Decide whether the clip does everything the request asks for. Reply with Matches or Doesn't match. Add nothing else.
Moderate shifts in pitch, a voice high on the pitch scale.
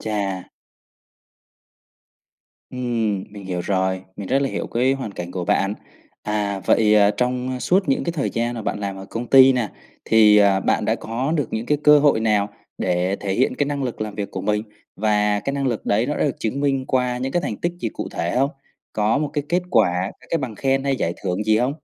Doesn't match